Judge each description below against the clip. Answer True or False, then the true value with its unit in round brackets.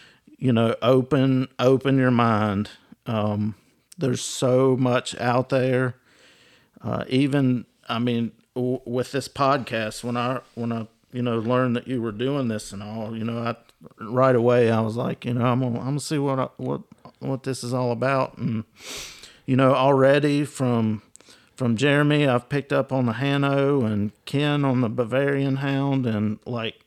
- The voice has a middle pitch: False (125 Hz)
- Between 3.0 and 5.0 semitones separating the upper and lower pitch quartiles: False (2.6 semitones)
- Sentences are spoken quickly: False (175 wpm)